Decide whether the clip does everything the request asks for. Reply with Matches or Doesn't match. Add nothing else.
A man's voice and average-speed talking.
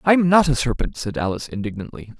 Matches